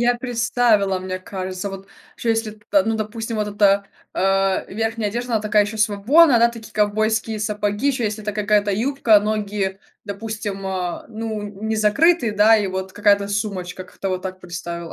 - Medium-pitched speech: No, high, 210 Hz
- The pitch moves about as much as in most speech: No, narrow, 2.3 semitones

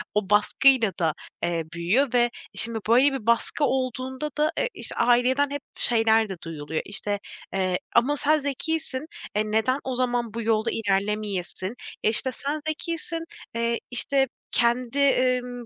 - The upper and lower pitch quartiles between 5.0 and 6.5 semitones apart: No, average, 4.1 semitones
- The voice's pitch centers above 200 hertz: Yes, high, 240 Hz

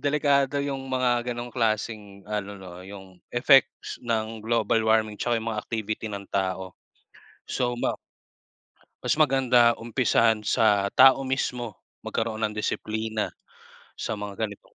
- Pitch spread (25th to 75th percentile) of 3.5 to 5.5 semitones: No, average, 2.8 semitones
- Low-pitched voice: Yes, low, 110 Hz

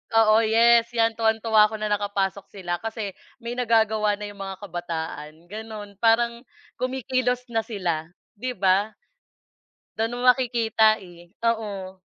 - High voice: Yes, high, 220 Hz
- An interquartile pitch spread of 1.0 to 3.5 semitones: Yes, average, 2.8 semitones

